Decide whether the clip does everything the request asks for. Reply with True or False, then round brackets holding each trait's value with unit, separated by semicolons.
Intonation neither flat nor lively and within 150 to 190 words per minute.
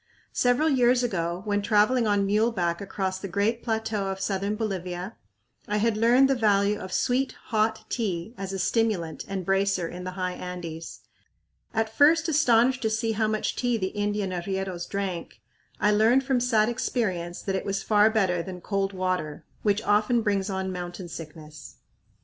True (3.4 semitones; 170 wpm)